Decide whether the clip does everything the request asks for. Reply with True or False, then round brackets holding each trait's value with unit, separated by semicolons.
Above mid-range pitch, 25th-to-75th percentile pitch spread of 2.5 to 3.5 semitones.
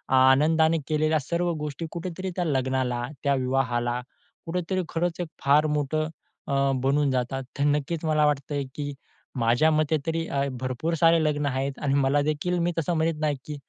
False (150 Hz; 3.1 semitones)